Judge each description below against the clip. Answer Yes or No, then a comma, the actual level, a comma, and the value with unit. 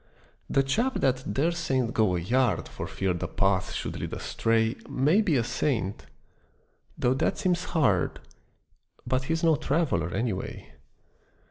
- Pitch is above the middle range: No, low, 130 Hz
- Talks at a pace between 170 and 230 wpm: No, average, 145 wpm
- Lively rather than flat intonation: Yes, wide, 6.7 semitones